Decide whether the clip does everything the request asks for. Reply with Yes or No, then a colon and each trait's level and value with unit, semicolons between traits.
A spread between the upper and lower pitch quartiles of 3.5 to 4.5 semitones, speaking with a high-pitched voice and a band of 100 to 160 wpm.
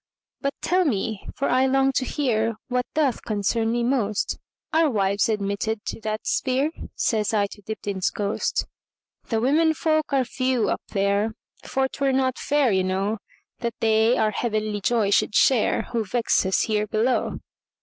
Yes: average, 3.9 semitones; high, 225 Hz; average, 145 wpm